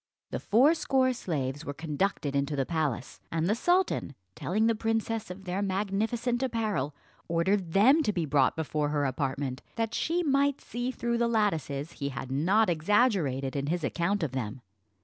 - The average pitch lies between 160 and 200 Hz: Yes, medium, 185 Hz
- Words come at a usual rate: Yes, average, 170 wpm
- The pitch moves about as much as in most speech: No, wide, 7.9 semitones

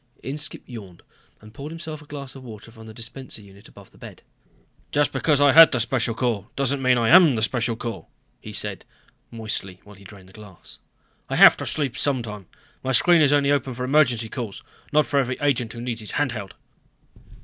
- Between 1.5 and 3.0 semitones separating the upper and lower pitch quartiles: No, average, 4.4 semitones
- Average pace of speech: No, fast, 210 wpm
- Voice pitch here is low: Yes, low, 125 Hz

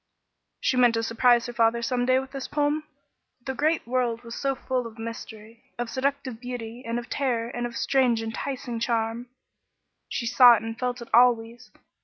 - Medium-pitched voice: No, high, 240 Hz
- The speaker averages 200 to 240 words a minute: No, average, 175 wpm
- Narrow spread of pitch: Yes, narrow, 2.0 semitones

